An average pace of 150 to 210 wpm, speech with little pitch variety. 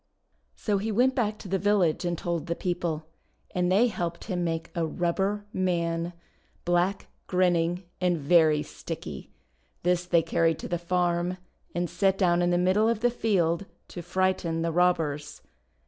Yes: average, 165 wpm; narrow, 2.0 semitones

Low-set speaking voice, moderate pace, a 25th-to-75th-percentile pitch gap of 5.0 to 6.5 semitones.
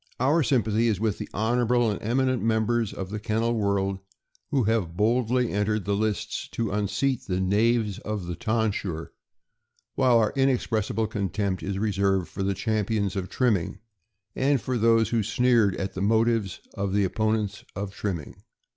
No: low, 110 Hz; average, 165 wpm; average, 2.9 semitones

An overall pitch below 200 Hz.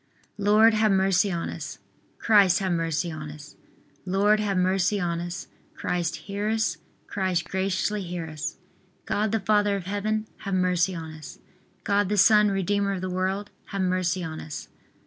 Yes: high, 190 Hz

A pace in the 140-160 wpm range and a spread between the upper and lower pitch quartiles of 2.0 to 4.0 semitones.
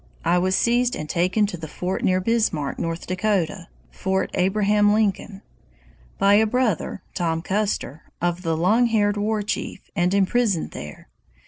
Yes: average, 150 wpm; average, 3.4 semitones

